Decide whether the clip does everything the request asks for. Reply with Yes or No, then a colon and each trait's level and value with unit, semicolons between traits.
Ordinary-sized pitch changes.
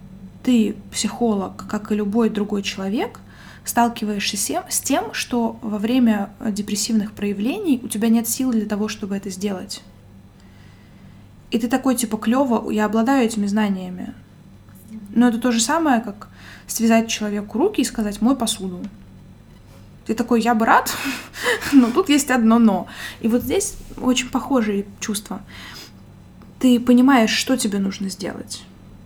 Yes: average, 3.2 semitones